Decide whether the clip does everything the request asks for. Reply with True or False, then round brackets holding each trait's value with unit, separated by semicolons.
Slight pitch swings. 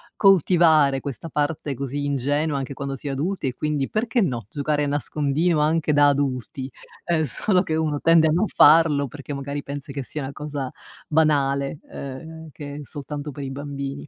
True (2.2 semitones)